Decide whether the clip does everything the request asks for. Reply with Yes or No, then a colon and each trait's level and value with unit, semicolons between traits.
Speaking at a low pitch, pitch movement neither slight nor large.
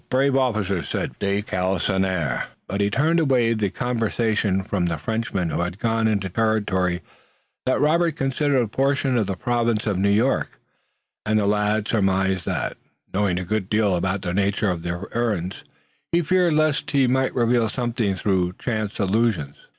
Yes: low, 105 Hz; average, 4.3 semitones